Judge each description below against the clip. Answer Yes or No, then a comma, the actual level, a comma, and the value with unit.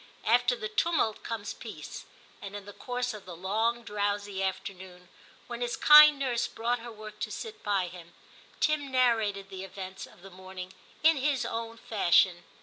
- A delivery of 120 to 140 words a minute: No, average, 170 wpm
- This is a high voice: Yes, high, 215 Hz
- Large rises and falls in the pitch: No, average, 4.2 semitones